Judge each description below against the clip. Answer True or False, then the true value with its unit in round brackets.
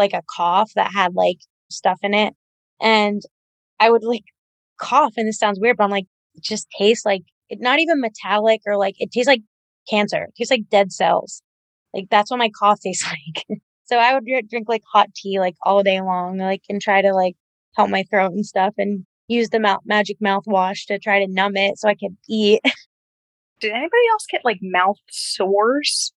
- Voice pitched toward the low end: False (205 Hz)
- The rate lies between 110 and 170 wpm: False (205 wpm)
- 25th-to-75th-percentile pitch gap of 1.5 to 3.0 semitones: True (2.6 semitones)